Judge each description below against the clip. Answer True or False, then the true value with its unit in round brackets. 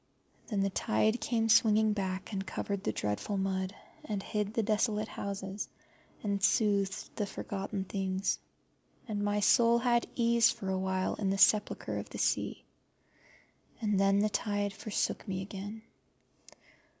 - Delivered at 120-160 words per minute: True (150 wpm)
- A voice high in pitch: True (205 Hz)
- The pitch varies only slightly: True (1.9 semitones)